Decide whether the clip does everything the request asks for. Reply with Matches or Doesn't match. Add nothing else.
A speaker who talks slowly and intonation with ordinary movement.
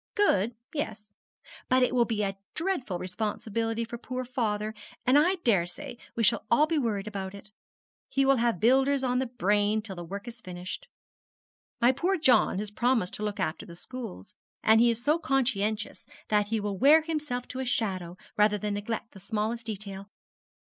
Doesn't match